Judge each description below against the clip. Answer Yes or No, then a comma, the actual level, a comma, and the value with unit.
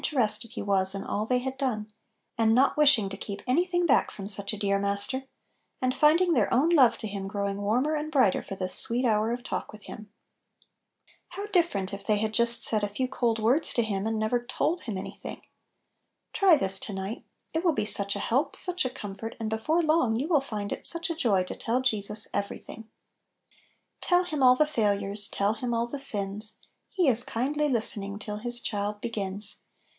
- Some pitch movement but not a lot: Yes, average, 4.8 semitones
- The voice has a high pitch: Yes, high, 225 Hz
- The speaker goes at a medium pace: No, fast, 215 wpm